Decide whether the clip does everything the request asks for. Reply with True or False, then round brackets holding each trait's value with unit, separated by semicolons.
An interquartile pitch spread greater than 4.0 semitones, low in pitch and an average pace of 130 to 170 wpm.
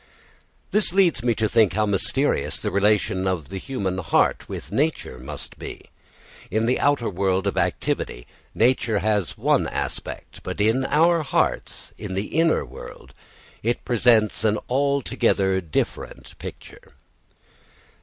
True (5.1 semitones; 110 Hz; 135 wpm)